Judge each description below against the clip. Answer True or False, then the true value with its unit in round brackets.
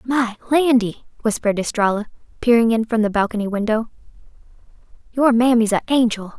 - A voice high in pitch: True (230 Hz)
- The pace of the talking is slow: True (130 wpm)